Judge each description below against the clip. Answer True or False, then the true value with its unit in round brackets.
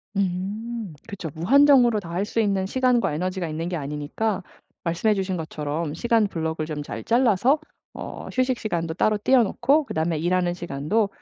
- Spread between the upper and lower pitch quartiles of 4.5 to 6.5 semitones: True (5.6 semitones)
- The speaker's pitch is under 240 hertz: True (190 Hz)